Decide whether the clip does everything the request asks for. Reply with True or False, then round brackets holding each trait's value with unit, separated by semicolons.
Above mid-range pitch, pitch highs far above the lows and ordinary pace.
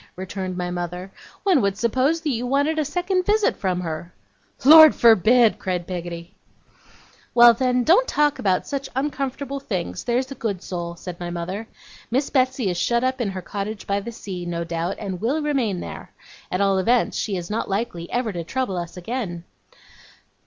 True (215 Hz; 6.5 semitones; 180 wpm)